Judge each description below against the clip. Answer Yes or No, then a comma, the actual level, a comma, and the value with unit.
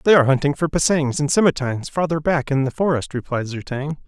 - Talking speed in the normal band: No, fast, 220 wpm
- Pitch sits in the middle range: Yes, medium, 145 Hz